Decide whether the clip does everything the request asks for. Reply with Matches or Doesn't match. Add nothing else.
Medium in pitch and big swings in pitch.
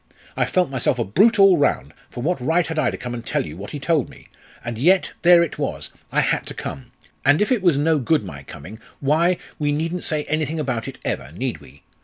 Matches